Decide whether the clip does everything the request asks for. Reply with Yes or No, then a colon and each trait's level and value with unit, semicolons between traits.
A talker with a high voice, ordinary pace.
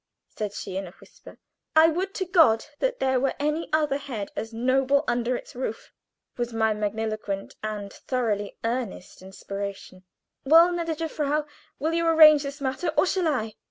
Yes: very high, 260 Hz; average, 165 wpm